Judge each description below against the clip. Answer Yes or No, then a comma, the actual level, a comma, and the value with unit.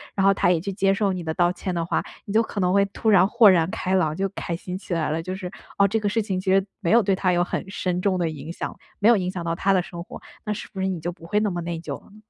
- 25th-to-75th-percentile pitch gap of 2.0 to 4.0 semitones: Yes, narrow, 2.4 semitones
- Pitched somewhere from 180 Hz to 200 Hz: Yes, medium, 185 Hz